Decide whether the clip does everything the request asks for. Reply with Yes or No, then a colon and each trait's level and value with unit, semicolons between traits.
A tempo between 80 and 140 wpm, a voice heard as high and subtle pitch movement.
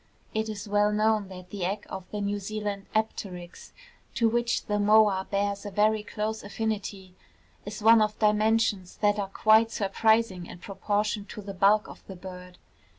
No: average, 170 wpm; high, 205 Hz; narrow, 1.7 semitones